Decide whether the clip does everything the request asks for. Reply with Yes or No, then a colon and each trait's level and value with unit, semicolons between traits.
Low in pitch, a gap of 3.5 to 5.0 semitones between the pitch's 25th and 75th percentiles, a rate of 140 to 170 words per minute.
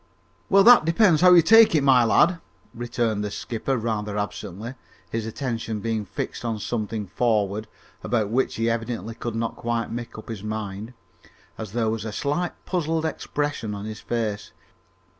Yes: low, 115 Hz; average, 3.8 semitones; average, 165 wpm